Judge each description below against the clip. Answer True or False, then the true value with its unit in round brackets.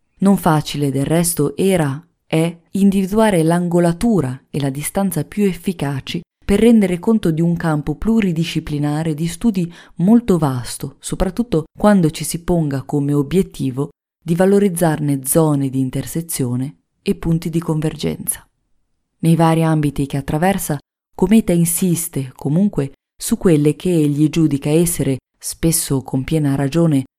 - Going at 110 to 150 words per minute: True (130 wpm)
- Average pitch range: True (4.0 semitones)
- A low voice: False (165 Hz)